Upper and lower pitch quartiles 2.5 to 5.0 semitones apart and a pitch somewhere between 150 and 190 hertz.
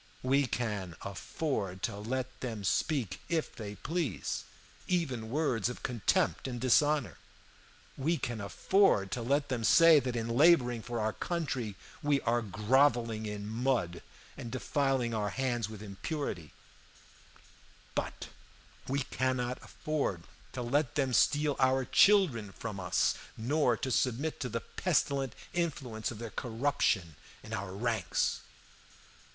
No: average, 4.5 semitones; low, 125 Hz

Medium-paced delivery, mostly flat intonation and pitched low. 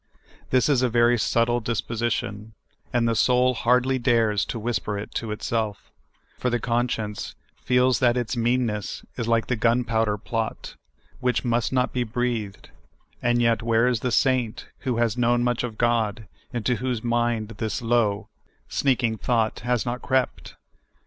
Yes: average, 160 wpm; narrow, 1.7 semitones; low, 120 Hz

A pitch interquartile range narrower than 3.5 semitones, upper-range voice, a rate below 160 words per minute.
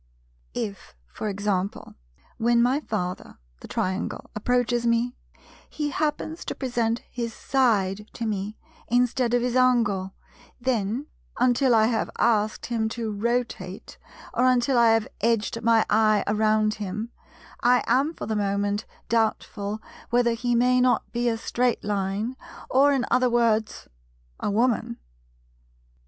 Yes: narrow, 2.6 semitones; high, 230 Hz; slow, 135 wpm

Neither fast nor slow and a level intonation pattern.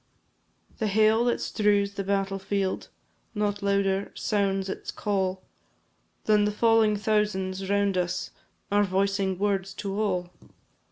No: slow, 125 wpm; narrow, 1.3 semitones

